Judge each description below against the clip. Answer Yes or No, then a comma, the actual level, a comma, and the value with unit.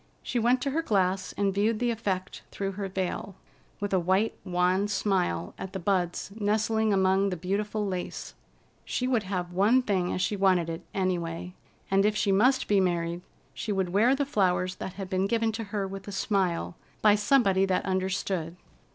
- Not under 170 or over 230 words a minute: Yes, average, 185 wpm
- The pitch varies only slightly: Yes, narrow, 2.3 semitones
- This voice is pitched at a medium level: No, high, 195 Hz